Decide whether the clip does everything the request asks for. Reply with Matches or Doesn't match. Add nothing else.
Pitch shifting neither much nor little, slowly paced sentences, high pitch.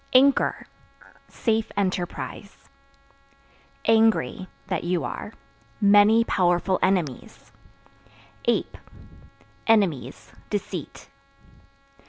Matches